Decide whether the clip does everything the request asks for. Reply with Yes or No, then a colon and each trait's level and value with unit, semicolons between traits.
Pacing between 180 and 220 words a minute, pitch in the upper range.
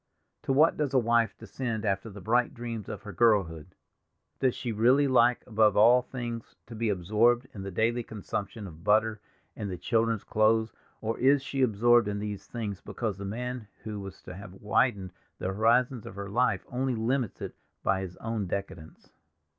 No: average, 185 wpm; low, 110 Hz